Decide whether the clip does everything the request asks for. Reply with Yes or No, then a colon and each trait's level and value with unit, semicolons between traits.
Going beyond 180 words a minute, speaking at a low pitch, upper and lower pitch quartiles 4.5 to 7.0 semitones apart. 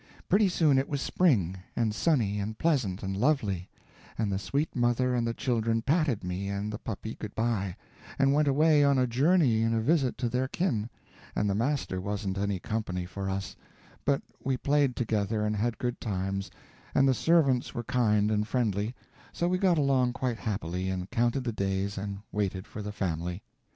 Yes: average, 190 wpm; low, 115 Hz; average, 5.1 semitones